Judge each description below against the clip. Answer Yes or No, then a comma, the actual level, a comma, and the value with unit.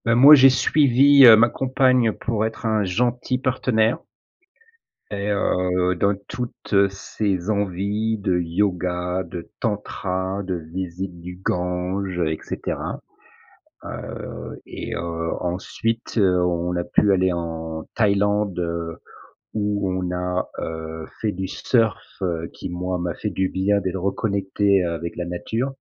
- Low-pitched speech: Yes, very low, 95 Hz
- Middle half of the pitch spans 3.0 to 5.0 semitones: Yes, average, 3.6 semitones